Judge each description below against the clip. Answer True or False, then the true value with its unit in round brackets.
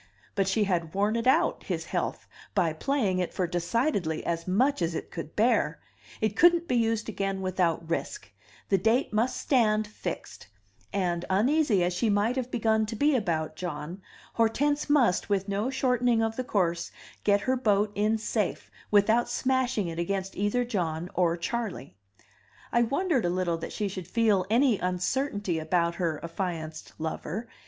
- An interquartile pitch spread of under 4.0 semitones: False (5.1 semitones)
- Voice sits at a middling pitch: False (205 Hz)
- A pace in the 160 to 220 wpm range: True (165 wpm)